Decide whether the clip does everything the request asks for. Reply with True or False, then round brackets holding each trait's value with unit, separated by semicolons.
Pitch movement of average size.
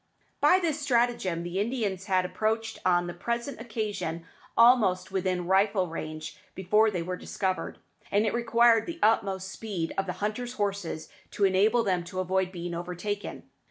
True (3.7 semitones)